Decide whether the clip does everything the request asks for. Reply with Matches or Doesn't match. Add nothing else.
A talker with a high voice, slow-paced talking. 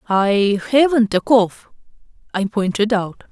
Matches